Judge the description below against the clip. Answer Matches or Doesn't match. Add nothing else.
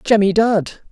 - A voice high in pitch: Matches